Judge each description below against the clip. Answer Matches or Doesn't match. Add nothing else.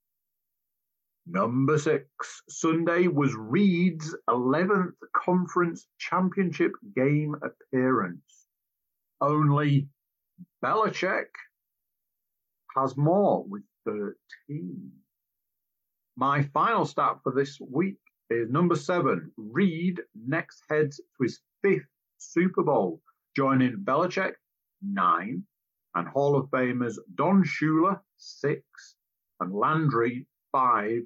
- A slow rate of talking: Matches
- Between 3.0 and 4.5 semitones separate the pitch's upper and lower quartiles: Doesn't match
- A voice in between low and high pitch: Matches